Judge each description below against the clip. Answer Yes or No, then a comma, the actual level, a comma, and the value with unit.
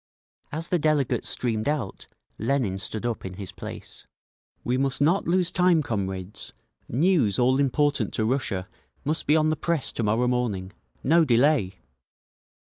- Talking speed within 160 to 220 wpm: No, average, 150 wpm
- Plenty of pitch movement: Yes, wide, 6.1 semitones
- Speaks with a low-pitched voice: Yes, low, 130 Hz